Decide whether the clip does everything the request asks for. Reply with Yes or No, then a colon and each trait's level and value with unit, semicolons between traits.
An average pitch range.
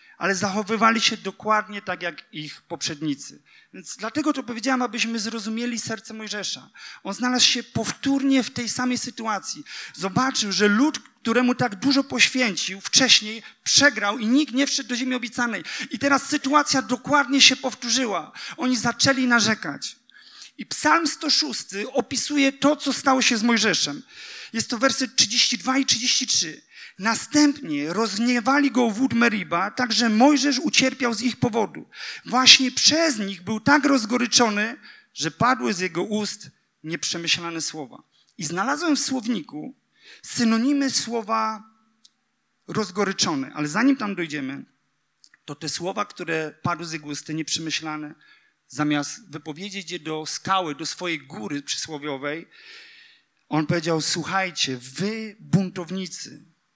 No: wide, 6.2 semitones